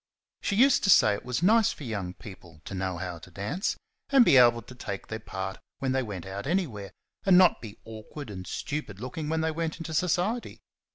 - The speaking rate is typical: No, fast, 215 wpm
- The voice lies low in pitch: Yes, low, 125 Hz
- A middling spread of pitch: No, wide, 8.9 semitones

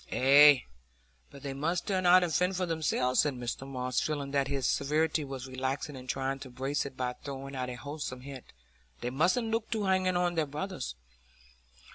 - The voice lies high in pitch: No, medium, 140 Hz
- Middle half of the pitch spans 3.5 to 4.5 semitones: Yes, average, 4.2 semitones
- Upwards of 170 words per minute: Yes, average, 190 wpm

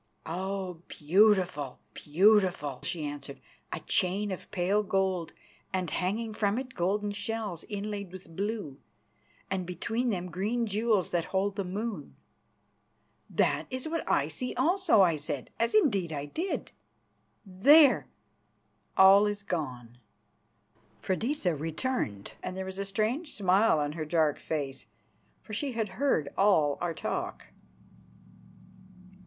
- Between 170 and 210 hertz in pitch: Yes, high, 190 Hz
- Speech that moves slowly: Yes, slow, 130 wpm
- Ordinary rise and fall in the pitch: Yes, average, 4.6 semitones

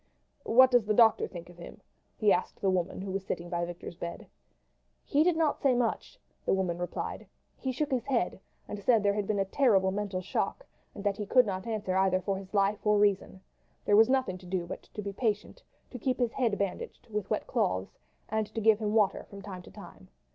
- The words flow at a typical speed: No, fast, 225 wpm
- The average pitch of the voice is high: Yes, high, 205 Hz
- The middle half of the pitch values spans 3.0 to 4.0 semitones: Yes, average, 3.4 semitones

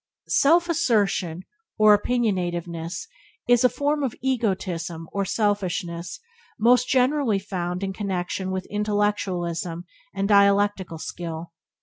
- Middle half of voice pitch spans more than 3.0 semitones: Yes, average, 4.3 semitones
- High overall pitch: Yes, high, 200 Hz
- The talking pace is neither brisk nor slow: No, slow, 105 wpm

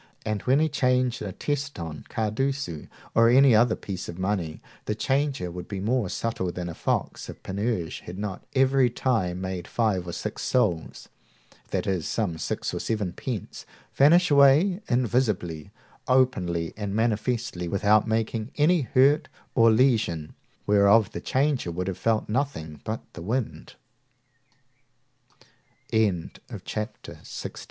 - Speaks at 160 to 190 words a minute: No, average, 140 wpm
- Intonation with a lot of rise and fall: Yes, wide, 6.0 semitones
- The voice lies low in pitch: Yes, low, 110 Hz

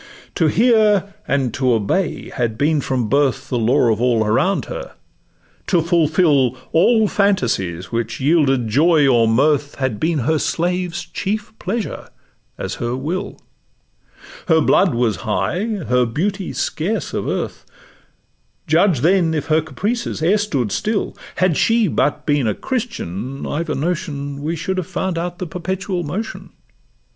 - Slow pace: No, average, 150 wpm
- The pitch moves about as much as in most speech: No, wide, 6.2 semitones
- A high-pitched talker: No, medium, 160 Hz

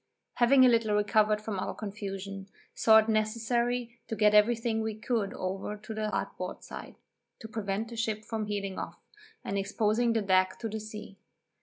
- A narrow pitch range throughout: Yes, narrow, 1.8 semitones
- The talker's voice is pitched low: No, high, 215 Hz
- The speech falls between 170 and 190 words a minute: Yes, average, 180 wpm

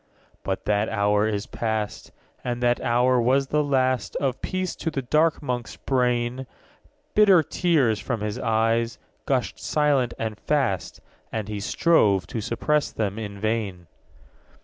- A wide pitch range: No, average, 4.1 semitones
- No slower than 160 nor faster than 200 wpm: No, average, 150 wpm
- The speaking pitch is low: Yes, low, 120 Hz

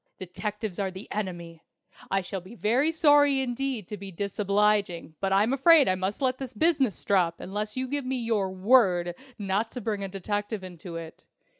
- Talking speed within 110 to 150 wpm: No, average, 180 wpm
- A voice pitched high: Yes, high, 205 Hz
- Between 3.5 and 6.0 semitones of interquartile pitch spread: Yes, average, 5.0 semitones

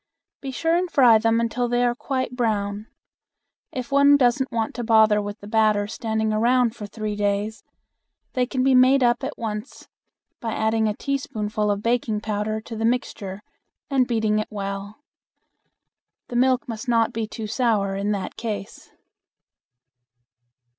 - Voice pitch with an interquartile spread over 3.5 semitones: No, average, 2.8 semitones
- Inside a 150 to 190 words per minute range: Yes, average, 160 wpm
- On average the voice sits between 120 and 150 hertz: No, high, 225 Hz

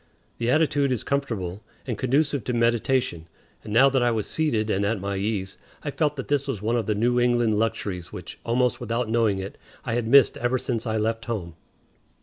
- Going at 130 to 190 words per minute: No, fast, 205 wpm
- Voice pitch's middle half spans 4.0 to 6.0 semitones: No, average, 3.4 semitones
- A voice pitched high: No, low, 115 Hz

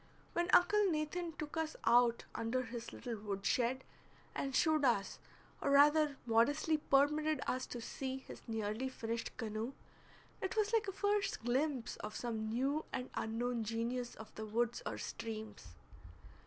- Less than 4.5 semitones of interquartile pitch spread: No, average, 5.1 semitones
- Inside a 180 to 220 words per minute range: No, average, 155 wpm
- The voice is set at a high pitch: Yes, very high, 250 Hz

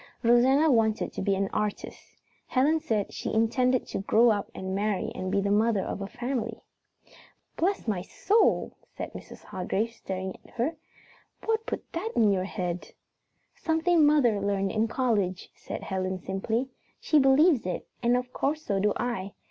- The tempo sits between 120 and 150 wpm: No, average, 165 wpm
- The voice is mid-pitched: No, high, 225 Hz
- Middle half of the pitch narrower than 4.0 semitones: No, average, 5.2 semitones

